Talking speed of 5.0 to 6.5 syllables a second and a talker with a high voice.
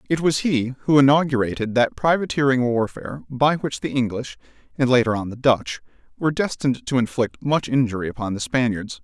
No: 5.7 syllables/s; low, 125 Hz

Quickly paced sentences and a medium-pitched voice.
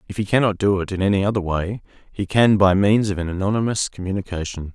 No: fast, 215 wpm; low, 100 Hz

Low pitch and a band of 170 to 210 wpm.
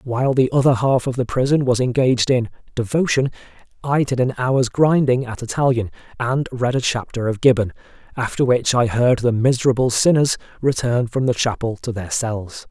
Yes: low, 125 Hz; average, 180 wpm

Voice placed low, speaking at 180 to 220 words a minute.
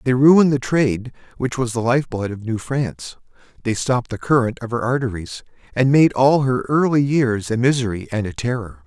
Yes: low, 125 Hz; fast, 205 wpm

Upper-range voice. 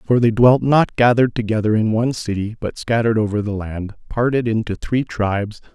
No: low, 110 Hz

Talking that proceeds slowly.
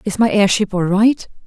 No: fast, 205 wpm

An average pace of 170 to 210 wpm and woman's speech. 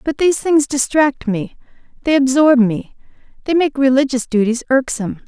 No: average, 150 wpm; female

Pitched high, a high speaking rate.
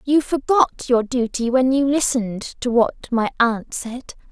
No: very high, 250 Hz; average, 165 wpm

